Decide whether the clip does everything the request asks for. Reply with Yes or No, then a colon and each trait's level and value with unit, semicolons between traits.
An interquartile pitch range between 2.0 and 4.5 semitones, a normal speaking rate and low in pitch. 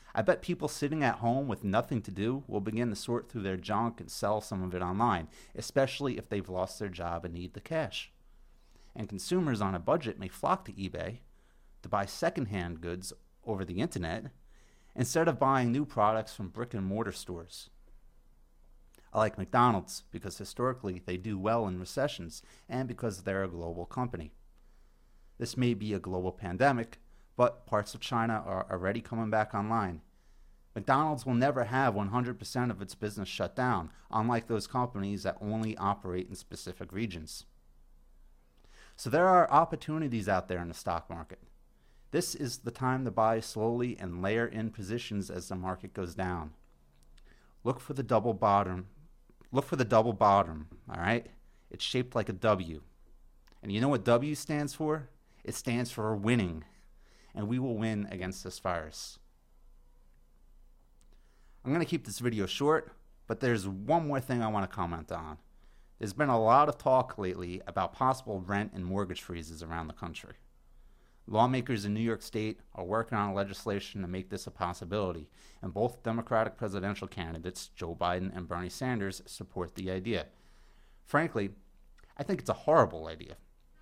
No: average, 5.0 semitones; average, 170 wpm; low, 100 Hz